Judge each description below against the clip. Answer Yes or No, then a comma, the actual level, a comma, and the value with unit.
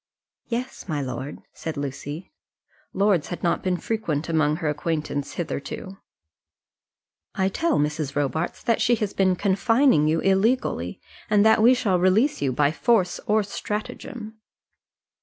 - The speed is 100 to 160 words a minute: Yes, average, 140 wpm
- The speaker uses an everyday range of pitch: No, wide, 6.2 semitones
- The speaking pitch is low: No, medium, 185 Hz